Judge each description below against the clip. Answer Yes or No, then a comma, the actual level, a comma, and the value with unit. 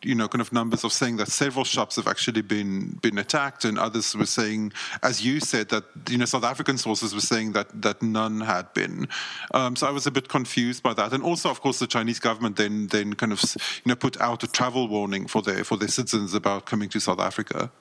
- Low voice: Yes, low, 115 Hz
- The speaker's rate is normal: No, fast, 245 wpm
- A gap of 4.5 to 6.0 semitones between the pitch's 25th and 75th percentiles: No, average, 2.8 semitones